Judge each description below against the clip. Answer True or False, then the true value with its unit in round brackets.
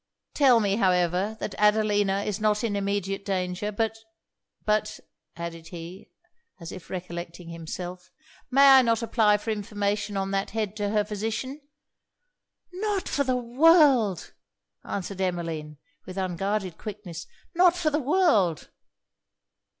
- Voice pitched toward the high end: True (205 Hz)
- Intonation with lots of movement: False (3.6 semitones)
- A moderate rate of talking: False (130 wpm)